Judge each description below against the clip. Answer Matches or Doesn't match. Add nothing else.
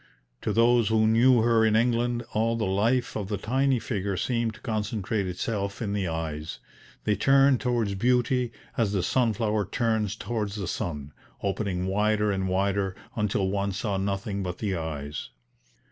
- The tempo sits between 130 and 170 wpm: Matches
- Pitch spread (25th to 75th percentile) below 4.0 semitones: Matches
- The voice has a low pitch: Matches